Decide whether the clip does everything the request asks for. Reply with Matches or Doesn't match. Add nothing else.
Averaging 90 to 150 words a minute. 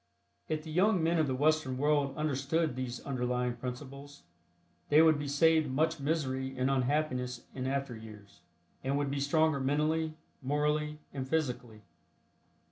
Matches